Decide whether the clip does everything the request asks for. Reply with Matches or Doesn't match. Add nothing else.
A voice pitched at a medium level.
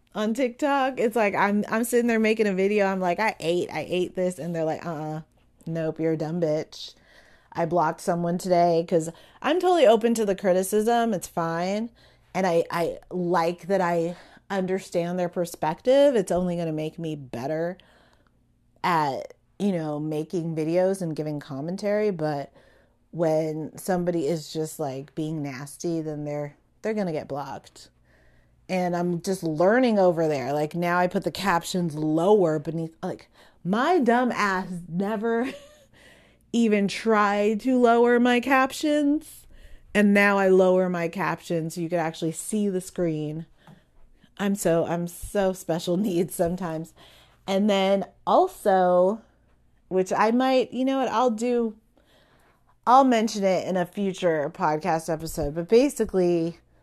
Matches